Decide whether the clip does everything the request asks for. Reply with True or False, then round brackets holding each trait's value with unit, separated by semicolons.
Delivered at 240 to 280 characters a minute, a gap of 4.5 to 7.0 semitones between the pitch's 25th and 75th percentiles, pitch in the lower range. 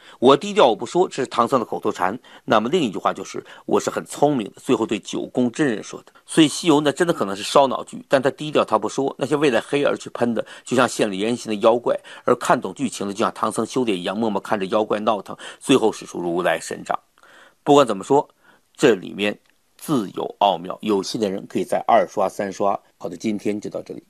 False (340 characters per minute; 5.4 semitones; 125 Hz)